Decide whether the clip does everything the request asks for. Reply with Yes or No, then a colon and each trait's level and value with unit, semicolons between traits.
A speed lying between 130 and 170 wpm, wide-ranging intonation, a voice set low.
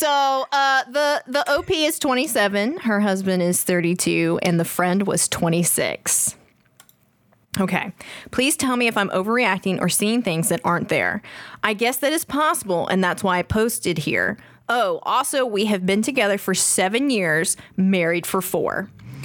No: average, 160 wpm; wide, 6.8 semitones; high, 200 Hz